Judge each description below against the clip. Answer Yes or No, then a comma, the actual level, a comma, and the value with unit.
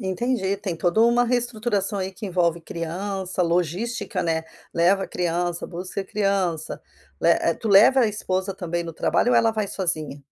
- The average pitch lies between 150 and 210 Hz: Yes, high, 190 Hz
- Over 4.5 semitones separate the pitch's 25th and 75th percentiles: No, average, 3.6 semitones